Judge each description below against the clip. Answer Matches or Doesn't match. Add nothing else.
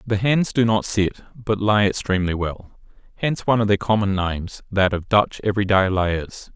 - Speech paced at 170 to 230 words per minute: Matches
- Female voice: Doesn't match